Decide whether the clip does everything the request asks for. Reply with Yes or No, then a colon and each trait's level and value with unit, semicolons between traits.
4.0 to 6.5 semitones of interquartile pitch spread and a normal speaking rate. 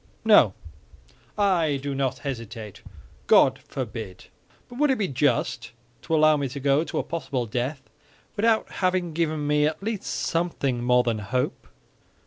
Yes: average, 5.3 semitones; average, 150 wpm